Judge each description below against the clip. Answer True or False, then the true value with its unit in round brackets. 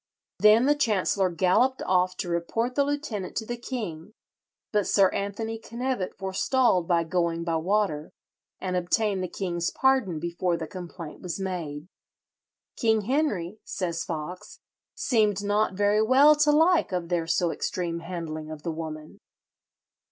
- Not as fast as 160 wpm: True (145 wpm)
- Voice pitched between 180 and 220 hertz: True (185 Hz)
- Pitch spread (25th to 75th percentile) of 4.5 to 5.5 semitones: True (4.8 semitones)